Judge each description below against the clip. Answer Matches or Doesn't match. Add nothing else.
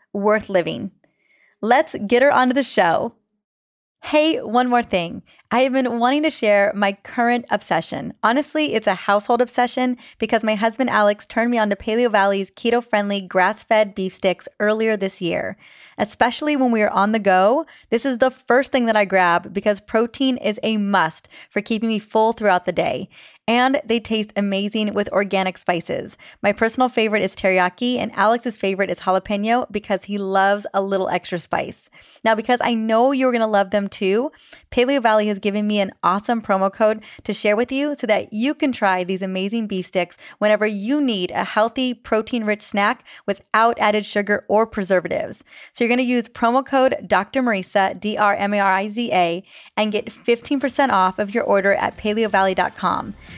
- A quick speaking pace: Doesn't match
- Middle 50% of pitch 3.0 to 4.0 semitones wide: Matches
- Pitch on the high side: Matches